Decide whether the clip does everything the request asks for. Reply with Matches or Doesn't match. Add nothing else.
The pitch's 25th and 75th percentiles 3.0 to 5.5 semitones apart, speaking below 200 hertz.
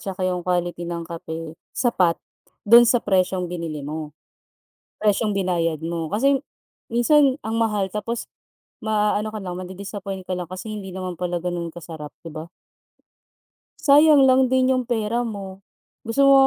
Matches